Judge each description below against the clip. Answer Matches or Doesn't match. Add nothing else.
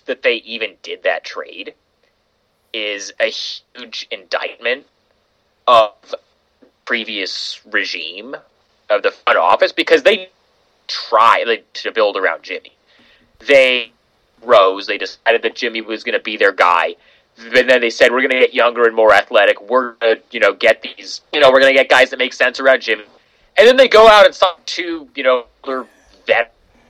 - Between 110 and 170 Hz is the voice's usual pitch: Matches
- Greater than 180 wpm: Doesn't match